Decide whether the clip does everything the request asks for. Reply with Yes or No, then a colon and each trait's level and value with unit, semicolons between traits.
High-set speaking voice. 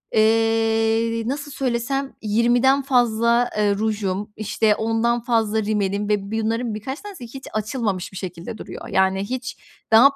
Yes: high, 225 Hz